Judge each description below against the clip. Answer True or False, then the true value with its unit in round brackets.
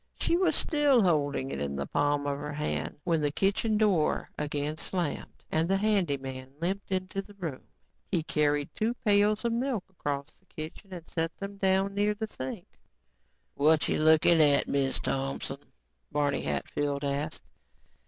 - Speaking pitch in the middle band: True (160 Hz)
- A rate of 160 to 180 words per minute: True (165 wpm)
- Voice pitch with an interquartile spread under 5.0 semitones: False (5.6 semitones)